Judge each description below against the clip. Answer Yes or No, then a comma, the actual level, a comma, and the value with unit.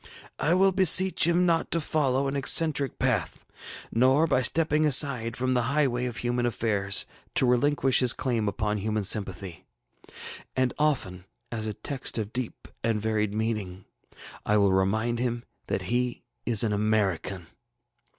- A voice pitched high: No, low, 120 Hz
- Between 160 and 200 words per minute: No, average, 150 wpm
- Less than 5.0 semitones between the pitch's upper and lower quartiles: Yes, average, 4.5 semitones